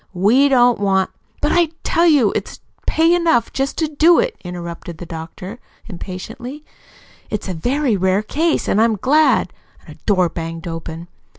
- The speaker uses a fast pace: No, average, 170 wpm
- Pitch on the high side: Yes, high, 220 Hz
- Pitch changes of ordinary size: No, wide, 8.6 semitones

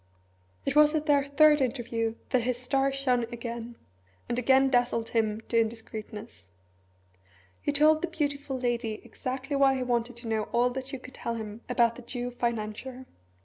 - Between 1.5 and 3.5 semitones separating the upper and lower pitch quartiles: Yes, average, 2.7 semitones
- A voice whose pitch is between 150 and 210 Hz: No, high, 245 Hz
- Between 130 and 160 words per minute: No, average, 170 wpm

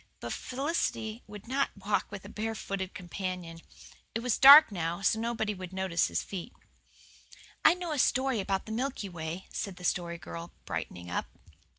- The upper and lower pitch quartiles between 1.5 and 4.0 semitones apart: No, average, 4.5 semitones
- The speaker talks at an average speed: Yes, average, 170 wpm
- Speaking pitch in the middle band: No, high, 200 Hz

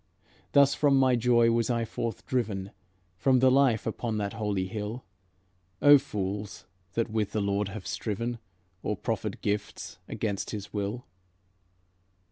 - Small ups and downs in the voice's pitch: No, average, 3.2 semitones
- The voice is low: Yes, low, 110 Hz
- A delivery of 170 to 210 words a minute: No, average, 140 wpm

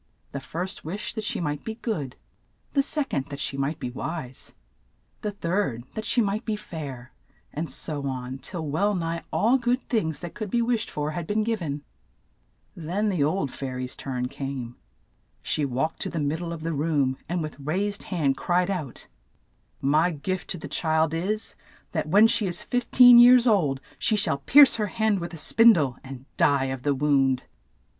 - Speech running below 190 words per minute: No, average, 195 wpm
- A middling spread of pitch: No, wide, 6.9 semitones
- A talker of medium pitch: Yes, medium, 165 Hz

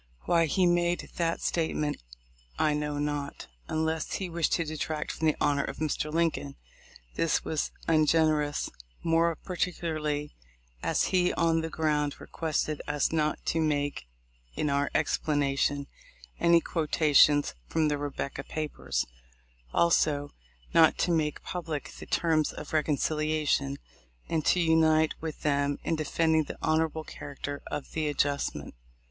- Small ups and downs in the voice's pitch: Yes, narrow, 1.9 semitones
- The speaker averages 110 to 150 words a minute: Yes, average, 140 wpm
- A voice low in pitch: No, medium, 155 Hz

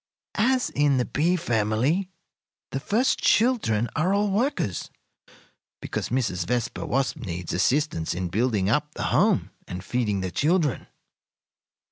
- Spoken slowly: Yes, slow, 130 wpm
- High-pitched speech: No, low, 130 Hz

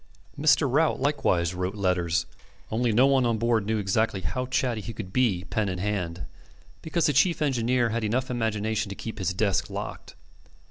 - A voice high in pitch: No, low, 110 Hz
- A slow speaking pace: No, average, 175 wpm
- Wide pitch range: No, average, 4.6 semitones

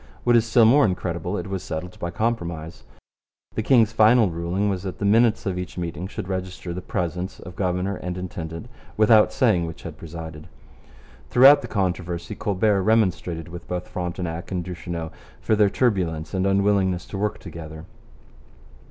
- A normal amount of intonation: Yes, average, 3.3 semitones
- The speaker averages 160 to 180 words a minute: Yes, average, 165 wpm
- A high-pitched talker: No, very low, 90 Hz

